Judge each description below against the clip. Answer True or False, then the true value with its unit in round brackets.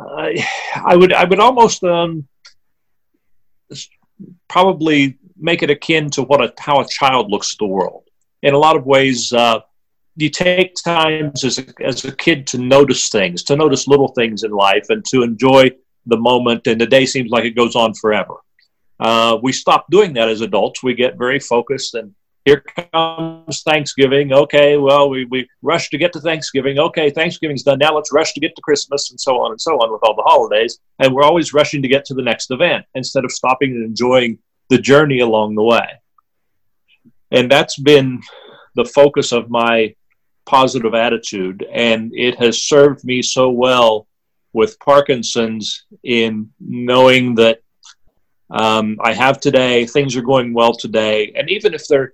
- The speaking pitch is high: False (135 Hz)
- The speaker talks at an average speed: True (180 wpm)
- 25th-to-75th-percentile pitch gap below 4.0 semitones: False (4.3 semitones)